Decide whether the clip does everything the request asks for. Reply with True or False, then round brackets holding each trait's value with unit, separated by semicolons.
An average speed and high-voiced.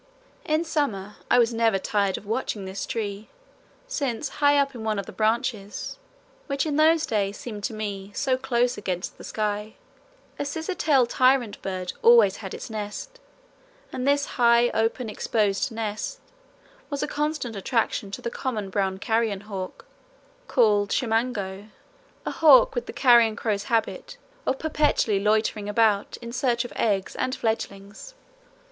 True (155 wpm; 225 Hz)